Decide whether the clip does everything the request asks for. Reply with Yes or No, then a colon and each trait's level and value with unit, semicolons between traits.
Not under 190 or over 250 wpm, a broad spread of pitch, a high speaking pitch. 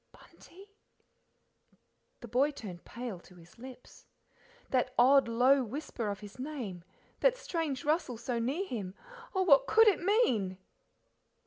No: slow, 135 wpm; wide, 5.7 semitones; very high, 255 Hz